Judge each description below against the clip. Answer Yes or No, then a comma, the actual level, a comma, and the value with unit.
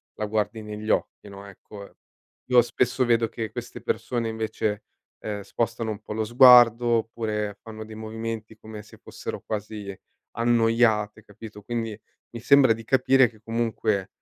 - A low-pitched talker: Yes, low, 110 Hz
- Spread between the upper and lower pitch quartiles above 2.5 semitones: No, narrow, 1.7 semitones